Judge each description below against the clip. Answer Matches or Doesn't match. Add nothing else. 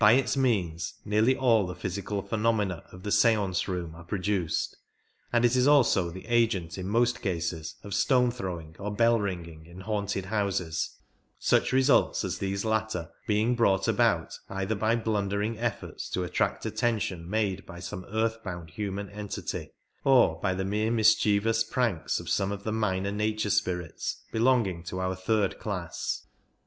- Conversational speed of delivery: Matches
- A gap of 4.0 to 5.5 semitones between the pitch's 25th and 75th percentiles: Doesn't match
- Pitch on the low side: Matches